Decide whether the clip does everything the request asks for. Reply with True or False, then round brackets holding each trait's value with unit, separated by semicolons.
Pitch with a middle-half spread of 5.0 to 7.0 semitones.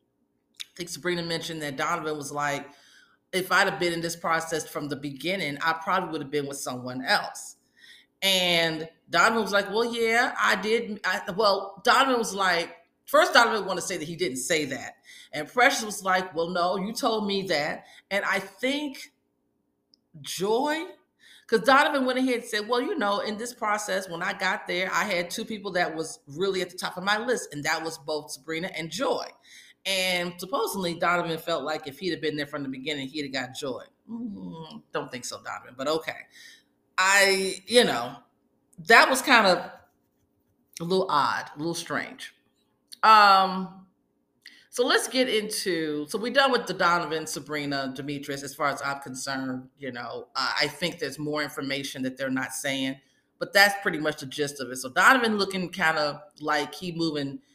True (5.4 semitones)